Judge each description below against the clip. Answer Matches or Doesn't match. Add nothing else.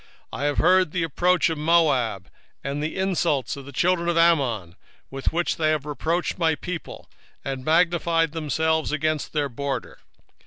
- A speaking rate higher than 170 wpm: Doesn't match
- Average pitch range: Matches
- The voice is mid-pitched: Matches